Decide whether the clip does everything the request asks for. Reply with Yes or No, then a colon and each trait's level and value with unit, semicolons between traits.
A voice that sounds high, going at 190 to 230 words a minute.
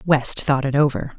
No: medium, 140 Hz; fast, 205 wpm